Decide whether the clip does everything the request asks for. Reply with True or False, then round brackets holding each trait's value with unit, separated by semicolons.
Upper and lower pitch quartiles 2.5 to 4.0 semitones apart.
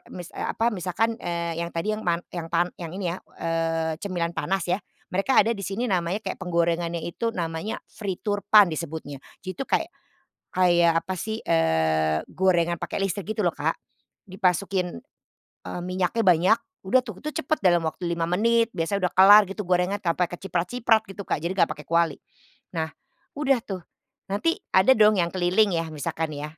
True (3.3 semitones)